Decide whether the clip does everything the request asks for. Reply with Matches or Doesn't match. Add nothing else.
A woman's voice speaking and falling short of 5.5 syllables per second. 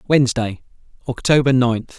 Doesn't match